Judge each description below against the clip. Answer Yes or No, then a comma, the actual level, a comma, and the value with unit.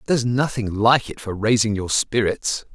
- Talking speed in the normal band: Yes, average, 175 wpm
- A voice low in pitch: Yes, low, 115 Hz